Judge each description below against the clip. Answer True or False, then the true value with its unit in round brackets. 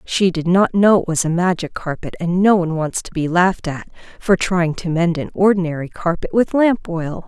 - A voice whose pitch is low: False (175 Hz)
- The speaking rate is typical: False (225 wpm)